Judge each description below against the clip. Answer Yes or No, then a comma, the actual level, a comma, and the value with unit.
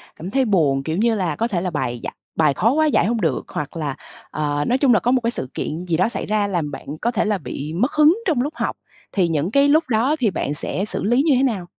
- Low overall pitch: No, high, 200 Hz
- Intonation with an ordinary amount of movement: No, wide, 7.5 semitones